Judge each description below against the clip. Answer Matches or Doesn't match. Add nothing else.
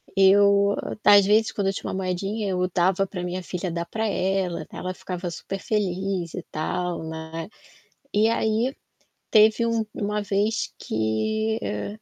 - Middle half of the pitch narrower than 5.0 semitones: Matches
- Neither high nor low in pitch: Doesn't match